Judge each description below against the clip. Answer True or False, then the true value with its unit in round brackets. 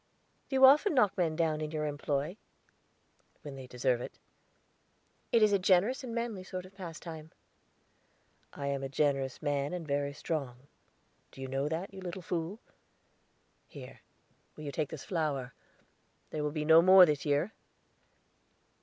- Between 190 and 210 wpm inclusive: False (160 wpm)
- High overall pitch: False (155 Hz)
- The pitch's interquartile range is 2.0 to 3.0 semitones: False (4.6 semitones)